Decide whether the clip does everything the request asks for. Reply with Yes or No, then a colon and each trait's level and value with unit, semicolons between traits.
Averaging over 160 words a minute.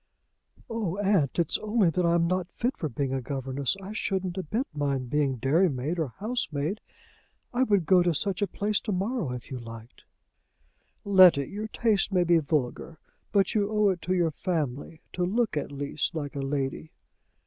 Yes: average, 180 wpm